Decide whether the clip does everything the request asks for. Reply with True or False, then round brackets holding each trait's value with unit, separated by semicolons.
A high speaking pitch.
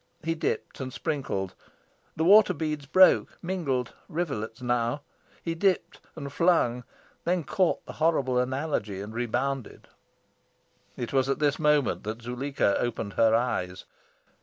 False (135 Hz)